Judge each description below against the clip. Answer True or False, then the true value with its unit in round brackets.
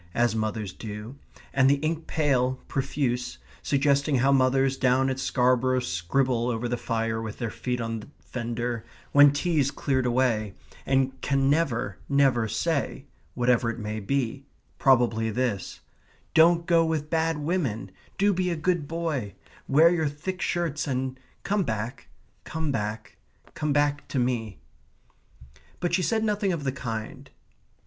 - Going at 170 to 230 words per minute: False (150 wpm)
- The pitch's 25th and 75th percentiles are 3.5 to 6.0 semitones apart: True (4.3 semitones)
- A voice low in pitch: True (130 Hz)